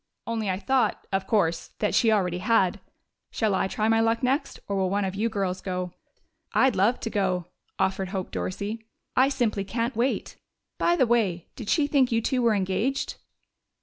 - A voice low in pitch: No, high, 210 Hz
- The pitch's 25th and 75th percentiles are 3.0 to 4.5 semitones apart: Yes, average, 3.8 semitones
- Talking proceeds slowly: No, average, 185 wpm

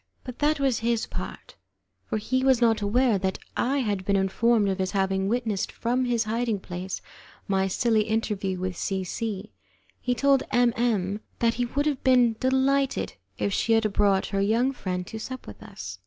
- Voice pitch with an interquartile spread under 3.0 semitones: No, average, 4.1 semitones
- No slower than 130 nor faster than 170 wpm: No, average, 185 wpm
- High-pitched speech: Yes, high, 225 Hz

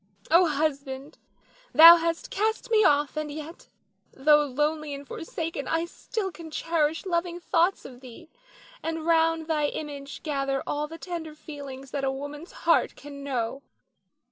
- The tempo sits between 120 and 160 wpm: Yes, average, 150 wpm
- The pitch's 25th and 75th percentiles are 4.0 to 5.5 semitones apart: No, average, 2.9 semitones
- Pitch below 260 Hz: No, very high, 305 Hz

